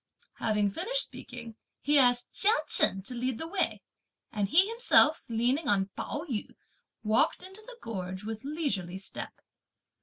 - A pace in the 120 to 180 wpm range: Yes, average, 150 wpm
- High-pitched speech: Yes, high, 245 Hz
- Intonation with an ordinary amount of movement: No, wide, 7.5 semitones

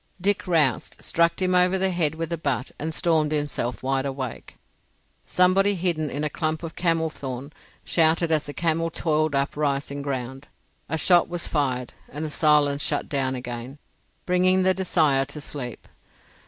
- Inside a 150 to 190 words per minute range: Yes, average, 170 wpm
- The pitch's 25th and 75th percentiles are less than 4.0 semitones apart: Yes, average, 3.4 semitones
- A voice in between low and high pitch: Yes, medium, 155 Hz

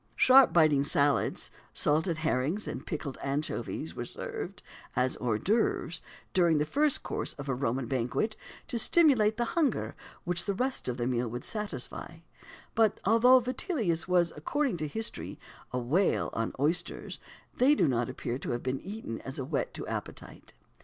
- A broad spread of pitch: Yes, wide, 8.7 semitones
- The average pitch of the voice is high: No, medium, 165 Hz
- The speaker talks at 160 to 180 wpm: Yes, average, 165 wpm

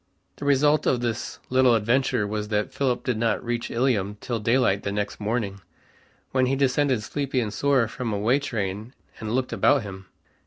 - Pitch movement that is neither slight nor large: Yes, average, 3.8 semitones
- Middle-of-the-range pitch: No, low, 120 Hz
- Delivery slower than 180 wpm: No, average, 185 wpm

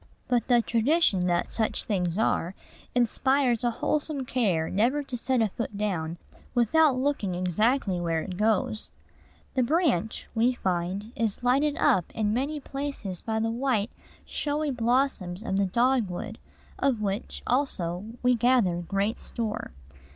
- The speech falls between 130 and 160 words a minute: Yes, average, 145 wpm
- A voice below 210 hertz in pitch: No, high, 225 Hz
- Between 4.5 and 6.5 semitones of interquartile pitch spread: Yes, average, 5.1 semitones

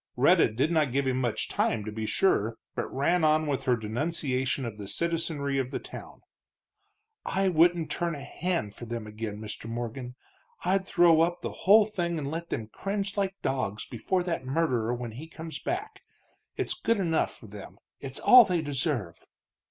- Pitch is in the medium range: Yes, medium, 145 Hz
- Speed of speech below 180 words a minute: No, average, 185 wpm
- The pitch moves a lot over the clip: Yes, wide, 6.4 semitones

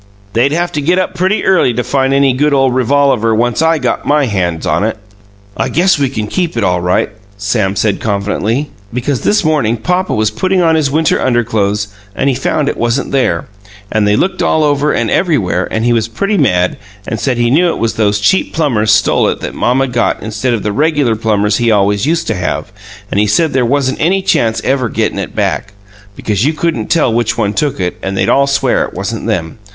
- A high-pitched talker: No, low, 125 Hz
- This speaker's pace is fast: Yes, fast, 220 wpm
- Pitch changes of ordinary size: No, wide, 5.8 semitones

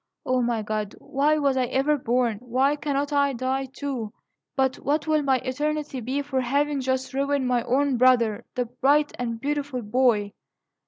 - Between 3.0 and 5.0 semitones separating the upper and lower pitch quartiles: No, narrow, 2.5 semitones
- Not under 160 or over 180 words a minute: Yes, average, 170 wpm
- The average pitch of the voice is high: Yes, very high, 265 Hz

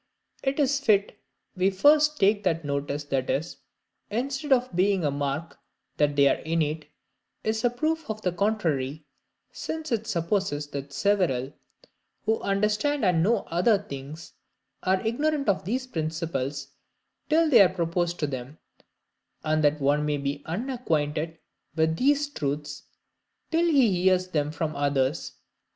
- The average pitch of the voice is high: No, medium, 175 Hz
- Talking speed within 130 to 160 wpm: Yes, average, 140 wpm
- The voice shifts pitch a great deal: Yes, wide, 7.3 semitones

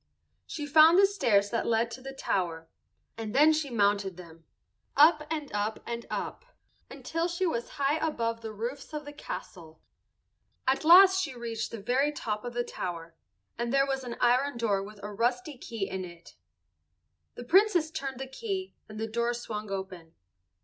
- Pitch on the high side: Yes, high, 240 Hz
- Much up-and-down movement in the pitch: Yes, wide, 6.0 semitones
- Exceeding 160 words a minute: Yes, average, 175 wpm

